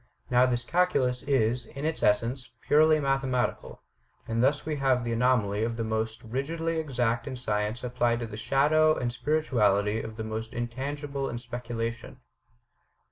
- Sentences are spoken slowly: No, average, 155 wpm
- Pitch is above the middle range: No, low, 125 Hz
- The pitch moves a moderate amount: Yes, average, 3.3 semitones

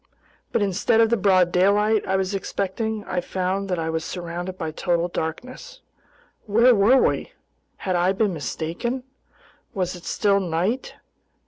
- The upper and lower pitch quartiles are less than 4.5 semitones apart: Yes, average, 3.3 semitones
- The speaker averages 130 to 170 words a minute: Yes, average, 150 wpm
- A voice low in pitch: No, high, 190 Hz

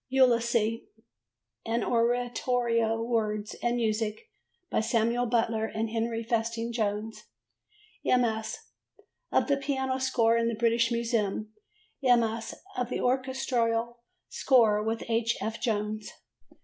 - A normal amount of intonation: No, narrow, 1.6 semitones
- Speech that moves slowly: Yes, slow, 110 wpm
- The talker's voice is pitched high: Yes, high, 230 Hz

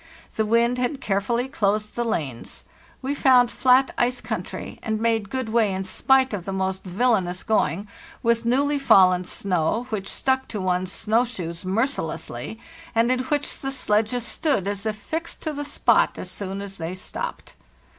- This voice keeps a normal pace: Yes, average, 170 wpm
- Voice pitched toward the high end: Yes, high, 220 Hz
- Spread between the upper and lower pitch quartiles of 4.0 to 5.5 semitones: Yes, average, 4.8 semitones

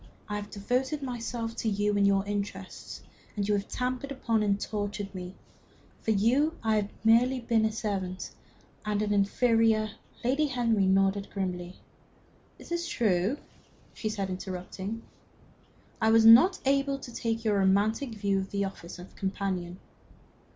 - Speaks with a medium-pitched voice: No, high, 210 Hz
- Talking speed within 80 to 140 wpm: No, average, 155 wpm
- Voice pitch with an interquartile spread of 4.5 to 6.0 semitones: No, average, 2.9 semitones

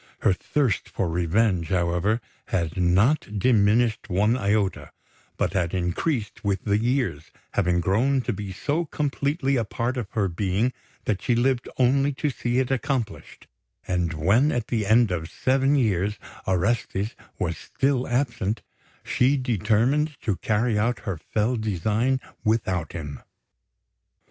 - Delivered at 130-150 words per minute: Yes, average, 140 wpm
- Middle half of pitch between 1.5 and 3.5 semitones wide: No, average, 5.1 semitones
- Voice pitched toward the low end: Yes, low, 110 Hz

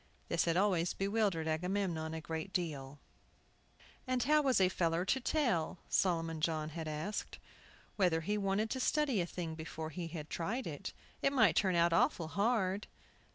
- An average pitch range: Yes, average, 4.4 semitones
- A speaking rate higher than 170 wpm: No, average, 160 wpm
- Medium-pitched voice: Yes, medium, 180 Hz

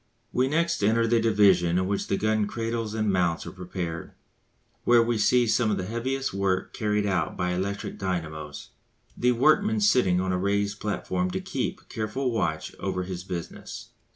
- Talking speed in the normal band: Yes, average, 175 wpm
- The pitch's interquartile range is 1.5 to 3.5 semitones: No, average, 4.1 semitones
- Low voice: Yes, low, 100 Hz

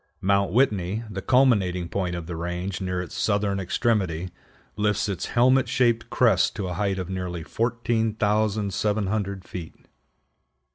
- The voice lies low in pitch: Yes, low, 100 Hz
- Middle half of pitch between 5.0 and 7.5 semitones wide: No, average, 3.1 semitones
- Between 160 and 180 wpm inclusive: No, slow, 135 wpm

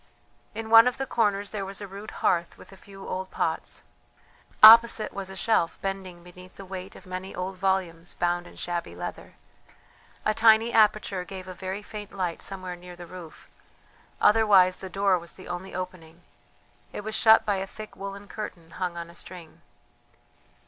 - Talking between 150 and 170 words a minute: No, average, 180 wpm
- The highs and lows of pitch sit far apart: No, narrow, 2.4 semitones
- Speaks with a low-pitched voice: No, high, 190 Hz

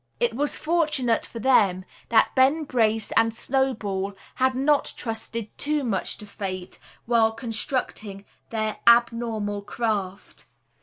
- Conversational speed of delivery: No, slow, 120 wpm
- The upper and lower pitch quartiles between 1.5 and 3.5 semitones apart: No, average, 3.9 semitones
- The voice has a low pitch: No, high, 230 Hz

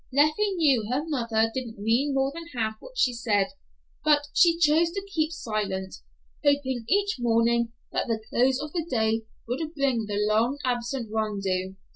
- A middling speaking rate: Yes, average, 165 wpm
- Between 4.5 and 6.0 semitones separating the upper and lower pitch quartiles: Yes, average, 5.1 semitones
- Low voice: No, high, 245 Hz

